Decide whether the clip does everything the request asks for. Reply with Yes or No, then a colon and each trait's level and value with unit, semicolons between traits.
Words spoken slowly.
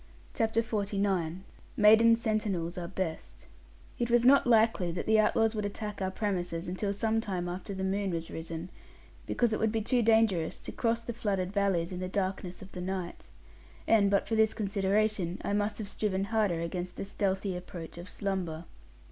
No: average, 180 wpm